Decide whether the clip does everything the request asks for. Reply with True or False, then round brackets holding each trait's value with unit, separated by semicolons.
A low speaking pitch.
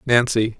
True (115 Hz)